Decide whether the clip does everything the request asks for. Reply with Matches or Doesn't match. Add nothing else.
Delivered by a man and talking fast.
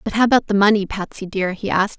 Doesn't match